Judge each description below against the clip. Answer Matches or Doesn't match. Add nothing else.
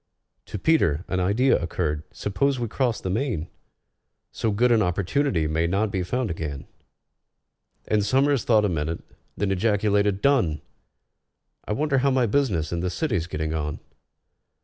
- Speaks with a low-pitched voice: Matches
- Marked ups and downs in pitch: Matches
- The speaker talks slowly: Doesn't match